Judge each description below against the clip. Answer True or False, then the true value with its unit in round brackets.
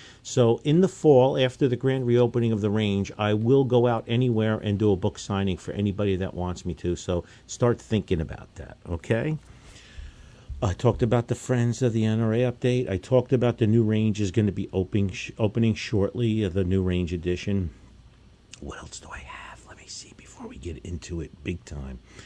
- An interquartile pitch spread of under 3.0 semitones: False (4.2 semitones)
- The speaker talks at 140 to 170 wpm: False (200 wpm)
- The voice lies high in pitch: False (110 Hz)